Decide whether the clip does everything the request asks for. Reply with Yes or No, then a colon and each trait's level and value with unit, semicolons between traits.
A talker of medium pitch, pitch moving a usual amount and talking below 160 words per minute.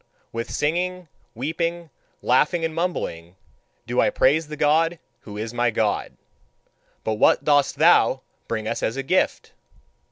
No: medium, 145 Hz; wide, 6.3 semitones; average, 140 wpm